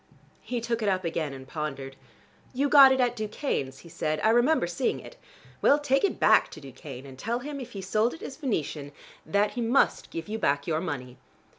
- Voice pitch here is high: Yes, high, 205 Hz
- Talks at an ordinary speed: No, fast, 210 wpm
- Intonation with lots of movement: Yes, wide, 8.8 semitones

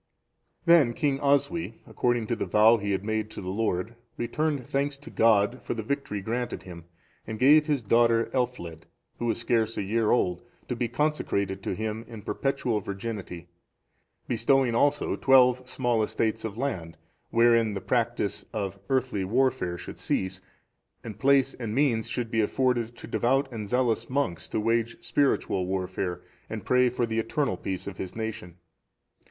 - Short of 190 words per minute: Yes, average, 165 wpm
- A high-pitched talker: No, low, 115 Hz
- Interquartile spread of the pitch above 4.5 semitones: No, average, 3.7 semitones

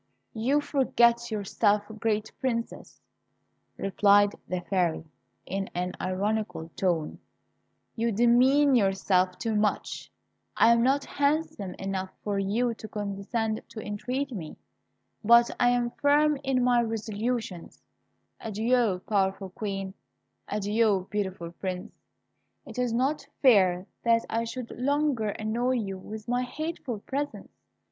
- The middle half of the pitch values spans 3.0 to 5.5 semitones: Yes, average, 3.9 semitones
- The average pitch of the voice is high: Yes, high, 220 Hz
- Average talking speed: No, slow, 120 wpm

